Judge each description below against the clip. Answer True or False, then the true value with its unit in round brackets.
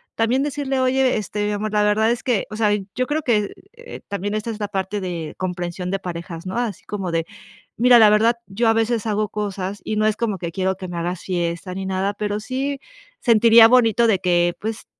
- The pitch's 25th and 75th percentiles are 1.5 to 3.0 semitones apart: False (3.6 semitones)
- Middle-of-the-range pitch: False (210 Hz)